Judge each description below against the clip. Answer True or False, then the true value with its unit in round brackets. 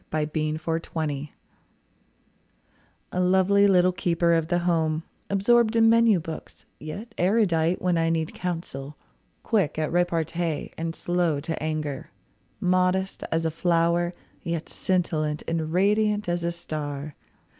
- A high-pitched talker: False (170 Hz)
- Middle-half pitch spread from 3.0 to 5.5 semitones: False (2.6 semitones)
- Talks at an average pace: False (130 wpm)